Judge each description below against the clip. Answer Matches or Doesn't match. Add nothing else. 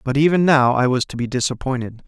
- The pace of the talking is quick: Matches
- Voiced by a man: Matches